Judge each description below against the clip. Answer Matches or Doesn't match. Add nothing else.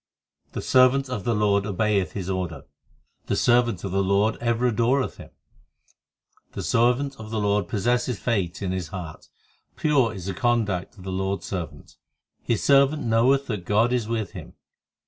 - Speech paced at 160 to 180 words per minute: Matches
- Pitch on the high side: Doesn't match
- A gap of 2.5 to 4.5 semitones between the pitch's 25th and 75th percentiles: Matches